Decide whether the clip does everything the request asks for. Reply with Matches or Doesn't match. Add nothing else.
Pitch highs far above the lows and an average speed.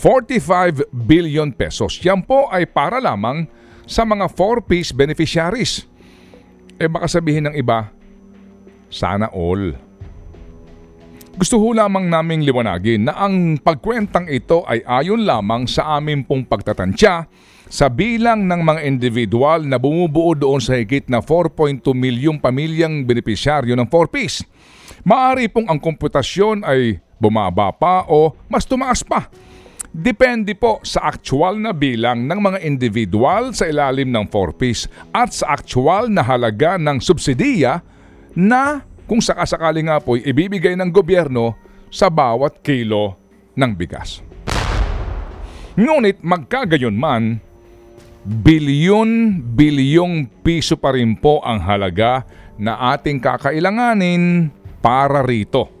Matches